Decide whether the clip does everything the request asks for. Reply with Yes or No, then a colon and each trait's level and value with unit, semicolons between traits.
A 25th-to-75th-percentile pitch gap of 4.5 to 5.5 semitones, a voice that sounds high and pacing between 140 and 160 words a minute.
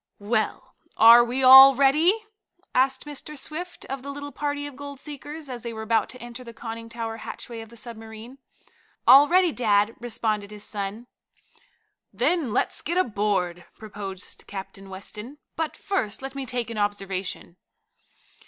Yes: average, 4.8 semitones; high, 235 Hz; average, 155 wpm